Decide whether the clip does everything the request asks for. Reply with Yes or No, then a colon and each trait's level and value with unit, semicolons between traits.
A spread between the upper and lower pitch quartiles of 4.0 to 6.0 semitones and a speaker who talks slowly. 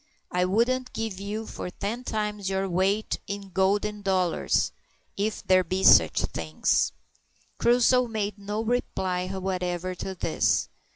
No: average, 2.7 semitones; slow, 130 wpm